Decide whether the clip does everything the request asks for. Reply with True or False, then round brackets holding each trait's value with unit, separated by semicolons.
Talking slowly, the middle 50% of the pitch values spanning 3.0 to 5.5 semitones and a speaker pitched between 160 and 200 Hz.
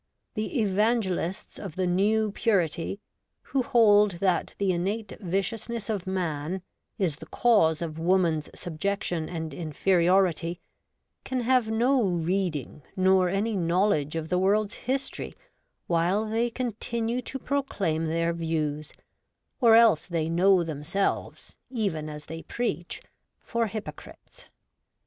True (120 wpm; 4.7 semitones; 190 Hz)